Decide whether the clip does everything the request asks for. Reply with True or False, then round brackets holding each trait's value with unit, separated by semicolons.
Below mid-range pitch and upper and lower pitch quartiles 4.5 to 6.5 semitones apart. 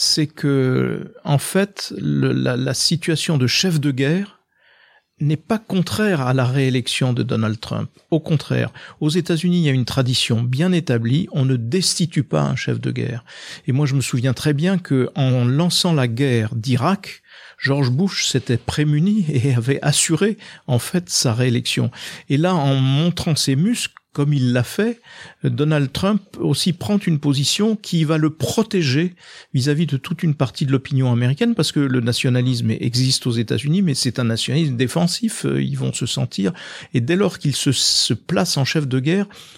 False (145 Hz; 5.2 semitones)